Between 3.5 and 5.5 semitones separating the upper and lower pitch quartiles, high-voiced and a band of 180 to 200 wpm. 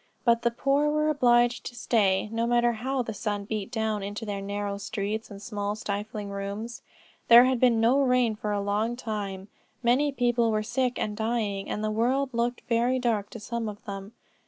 No: average, 2.8 semitones; high, 225 Hz; average, 195 wpm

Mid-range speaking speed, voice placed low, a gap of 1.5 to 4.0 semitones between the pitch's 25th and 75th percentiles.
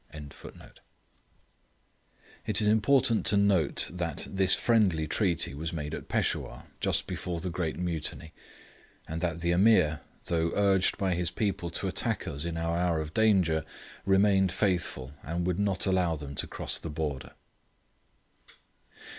Yes: average, 145 wpm; very low, 85 Hz; average, 3.4 semitones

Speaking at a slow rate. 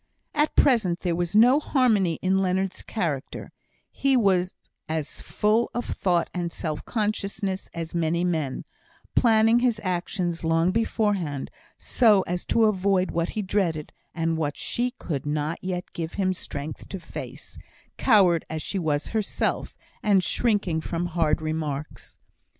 No: average, 145 wpm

